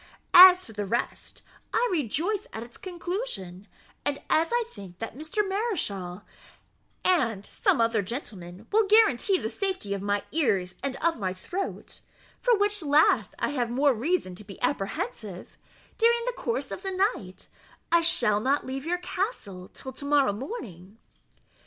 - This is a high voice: Yes, very high, 275 Hz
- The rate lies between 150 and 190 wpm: Yes, average, 160 wpm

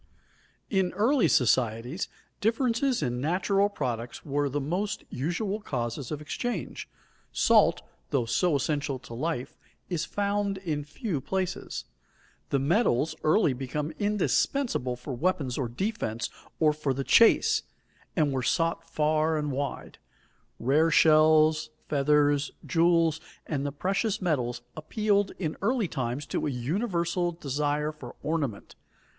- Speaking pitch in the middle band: Yes, medium, 155 Hz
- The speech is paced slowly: Yes, slow, 125 wpm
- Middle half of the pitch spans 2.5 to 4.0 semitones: No, average, 5.3 semitones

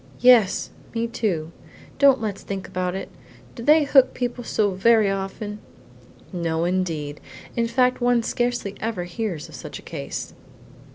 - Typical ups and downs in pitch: Yes, average, 4.8 semitones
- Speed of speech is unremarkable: Yes, average, 150 wpm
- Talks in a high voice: Yes, high, 210 Hz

